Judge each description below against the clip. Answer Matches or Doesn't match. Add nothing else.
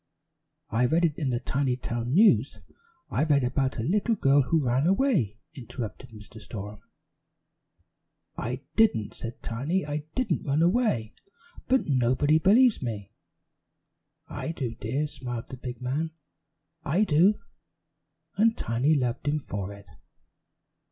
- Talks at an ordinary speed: Doesn't match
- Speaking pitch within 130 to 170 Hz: Matches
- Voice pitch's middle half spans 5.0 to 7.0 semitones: Matches